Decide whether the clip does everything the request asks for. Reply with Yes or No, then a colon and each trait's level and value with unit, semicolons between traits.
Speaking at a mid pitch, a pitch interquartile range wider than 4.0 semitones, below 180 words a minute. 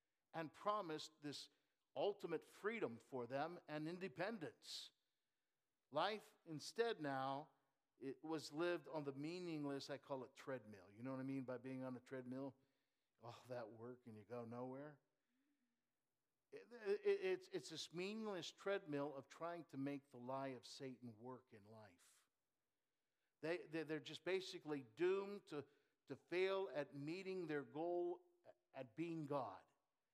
Yes: medium, 145 Hz; average, 4.9 semitones; average, 145 wpm